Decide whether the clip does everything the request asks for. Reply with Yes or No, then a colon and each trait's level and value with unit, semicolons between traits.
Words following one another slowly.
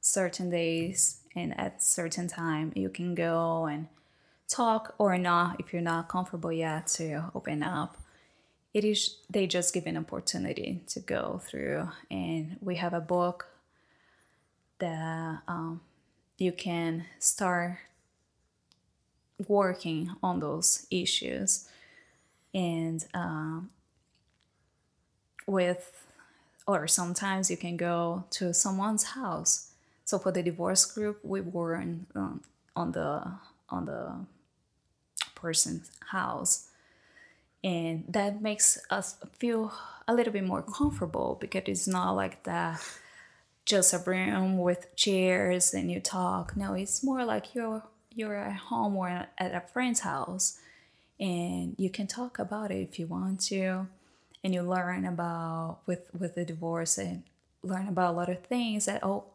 No: average, 135 wpm